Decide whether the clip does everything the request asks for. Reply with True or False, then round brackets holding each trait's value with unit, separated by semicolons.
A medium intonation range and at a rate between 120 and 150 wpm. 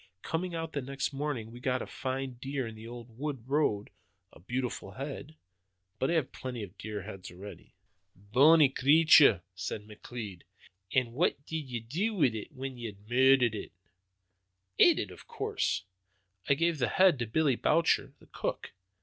False (4.6 semitones; 175 wpm)